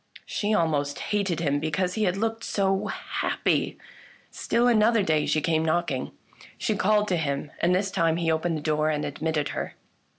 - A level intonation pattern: No, average, 4.6 semitones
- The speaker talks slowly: No, average, 175 wpm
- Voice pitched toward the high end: No, medium, 170 Hz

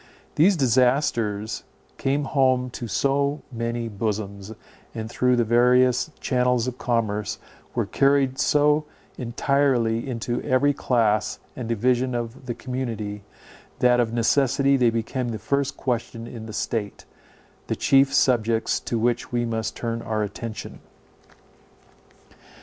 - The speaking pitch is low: Yes, low, 120 Hz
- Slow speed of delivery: Yes, slow, 125 wpm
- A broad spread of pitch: No, narrow, 2.6 semitones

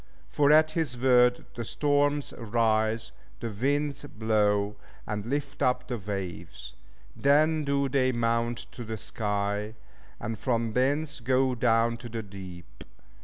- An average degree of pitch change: Yes, average, 4.4 semitones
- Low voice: Yes, low, 120 Hz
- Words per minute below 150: Yes, slow, 135 wpm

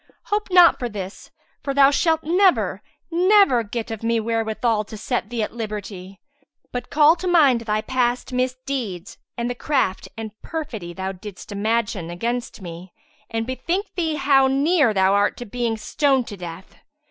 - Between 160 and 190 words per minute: Yes, average, 165 wpm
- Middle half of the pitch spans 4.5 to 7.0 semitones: Yes, average, 5.0 semitones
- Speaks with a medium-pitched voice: No, high, 235 Hz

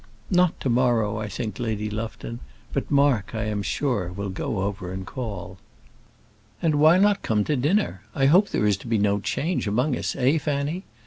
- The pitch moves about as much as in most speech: No, wide, 5.9 semitones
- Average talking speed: Yes, average, 190 wpm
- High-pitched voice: No, low, 115 Hz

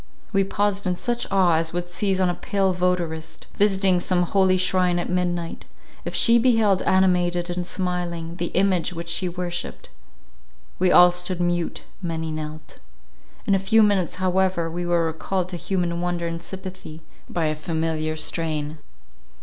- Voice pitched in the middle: Yes, medium, 175 Hz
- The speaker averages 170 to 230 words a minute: No, average, 160 wpm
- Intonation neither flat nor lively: No, narrow, 1.9 semitones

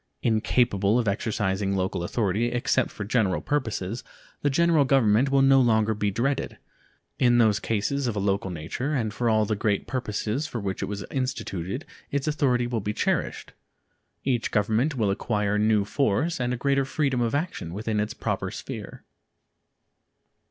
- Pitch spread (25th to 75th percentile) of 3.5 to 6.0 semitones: Yes, average, 4.2 semitones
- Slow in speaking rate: No, average, 165 wpm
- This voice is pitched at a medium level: No, low, 115 Hz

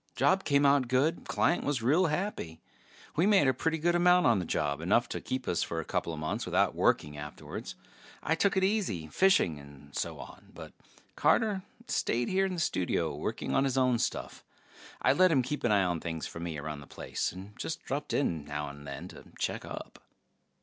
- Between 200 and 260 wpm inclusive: Yes, fast, 205 wpm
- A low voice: Yes, low, 125 Hz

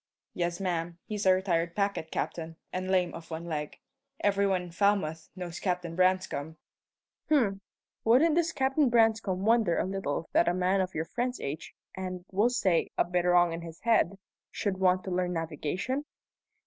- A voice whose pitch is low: No, medium, 185 Hz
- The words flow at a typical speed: Yes, average, 175 wpm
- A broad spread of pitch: No, average, 3.1 semitones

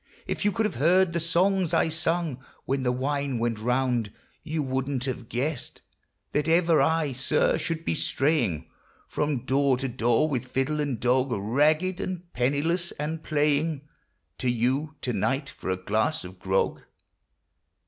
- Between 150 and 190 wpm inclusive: Yes, average, 160 wpm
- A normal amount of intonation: Yes, average, 4.4 semitones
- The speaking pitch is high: No, medium, 140 Hz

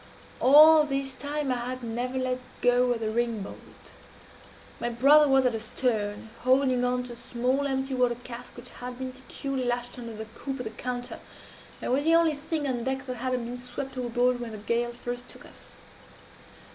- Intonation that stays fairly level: Yes, narrow, 1.8 semitones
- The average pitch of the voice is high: Yes, very high, 250 Hz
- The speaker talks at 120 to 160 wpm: No, average, 195 wpm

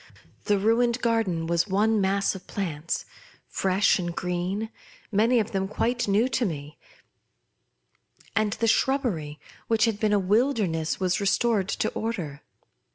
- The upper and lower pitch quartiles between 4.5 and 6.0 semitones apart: No, average, 4.1 semitones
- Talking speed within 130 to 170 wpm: Yes, average, 140 wpm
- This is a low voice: No, high, 200 Hz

